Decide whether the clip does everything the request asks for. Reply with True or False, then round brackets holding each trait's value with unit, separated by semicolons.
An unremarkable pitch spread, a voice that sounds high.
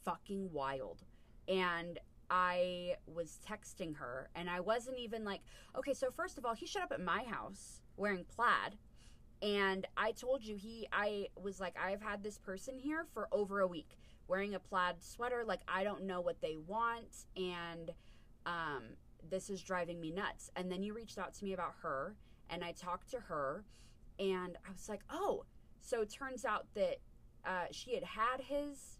True (4.5 semitones; 195 Hz)